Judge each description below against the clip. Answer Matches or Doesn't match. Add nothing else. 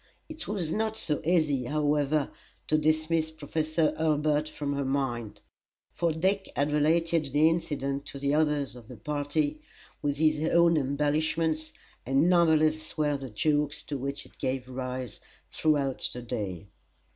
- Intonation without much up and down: Matches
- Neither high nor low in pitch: Matches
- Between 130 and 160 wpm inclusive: Matches